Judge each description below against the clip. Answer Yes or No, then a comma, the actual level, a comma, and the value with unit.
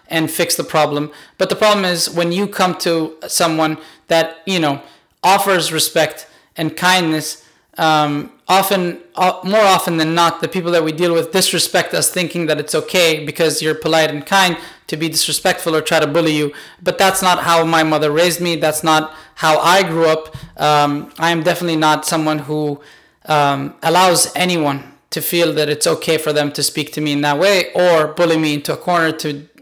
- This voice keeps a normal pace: Yes, average, 195 wpm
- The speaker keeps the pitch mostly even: Yes, narrow, 2.3 semitones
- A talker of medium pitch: Yes, medium, 160 Hz